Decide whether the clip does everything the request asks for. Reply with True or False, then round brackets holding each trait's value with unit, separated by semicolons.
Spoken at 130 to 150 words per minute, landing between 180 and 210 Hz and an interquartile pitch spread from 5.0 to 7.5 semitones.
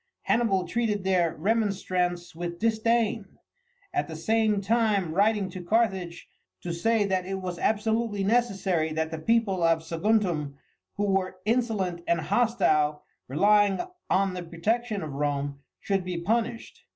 False (140 wpm; 190 Hz; 4.4 semitones)